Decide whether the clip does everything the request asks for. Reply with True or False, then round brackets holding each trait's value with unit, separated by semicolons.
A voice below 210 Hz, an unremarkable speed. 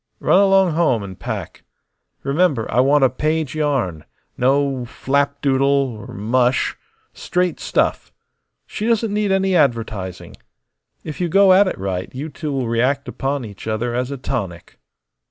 True (140 Hz; 150 wpm)